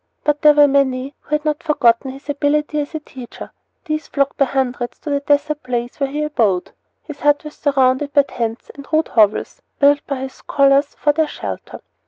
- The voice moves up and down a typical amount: No, narrow, 2.3 semitones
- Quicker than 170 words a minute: Yes, average, 200 wpm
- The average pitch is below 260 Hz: No, very high, 285 Hz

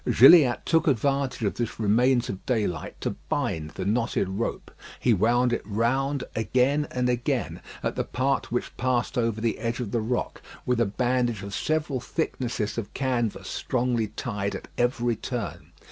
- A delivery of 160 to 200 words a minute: Yes, average, 165 wpm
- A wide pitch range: No, narrow, 2.6 semitones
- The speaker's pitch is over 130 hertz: No, low, 120 Hz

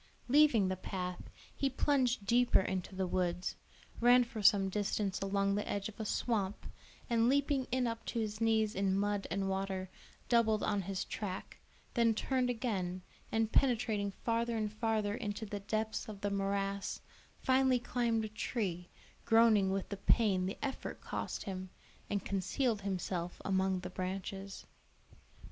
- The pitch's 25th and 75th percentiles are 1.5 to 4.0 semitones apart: Yes, average, 3.2 semitones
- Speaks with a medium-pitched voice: No, high, 205 Hz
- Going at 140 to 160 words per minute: Yes, average, 155 wpm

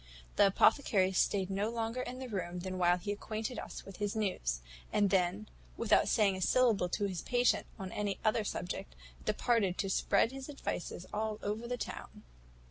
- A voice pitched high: Yes, high, 205 Hz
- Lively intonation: No, average, 3.3 semitones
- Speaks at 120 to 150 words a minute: No, average, 180 wpm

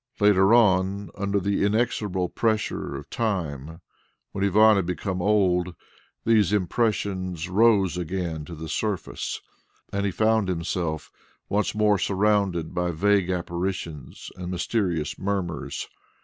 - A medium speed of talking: No, slow, 120 wpm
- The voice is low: Yes, very low, 95 Hz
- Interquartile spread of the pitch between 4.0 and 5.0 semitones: No, average, 2.8 semitones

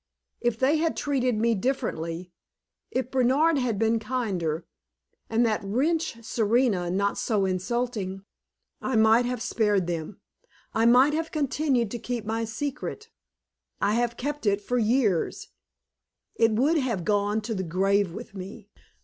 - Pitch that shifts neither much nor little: Yes, average, 4.1 semitones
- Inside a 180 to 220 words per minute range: No, average, 145 wpm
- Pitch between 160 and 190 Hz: No, high, 225 Hz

